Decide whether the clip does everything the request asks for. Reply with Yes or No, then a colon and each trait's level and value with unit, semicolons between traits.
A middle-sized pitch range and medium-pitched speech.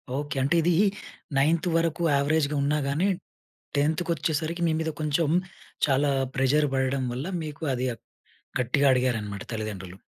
Yes: average, 3.3 semitones; medium, 145 Hz